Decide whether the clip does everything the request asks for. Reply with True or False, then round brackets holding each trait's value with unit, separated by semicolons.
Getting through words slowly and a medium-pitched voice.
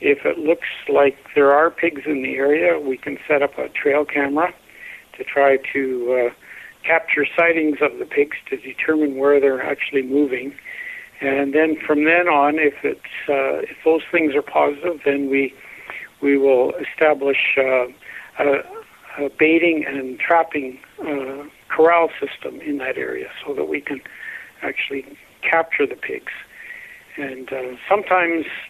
False (155 wpm; 150 Hz)